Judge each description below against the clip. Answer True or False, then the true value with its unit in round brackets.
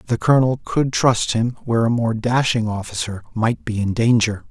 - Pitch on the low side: True (115 Hz)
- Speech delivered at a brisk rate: False (185 wpm)